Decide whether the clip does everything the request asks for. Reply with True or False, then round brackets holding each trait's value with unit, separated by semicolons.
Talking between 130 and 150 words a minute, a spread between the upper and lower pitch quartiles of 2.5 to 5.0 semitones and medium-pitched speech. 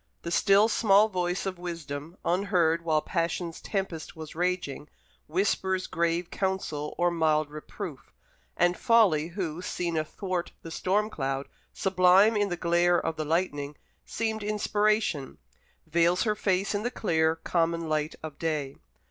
True (140 wpm; 3.3 semitones; 175 Hz)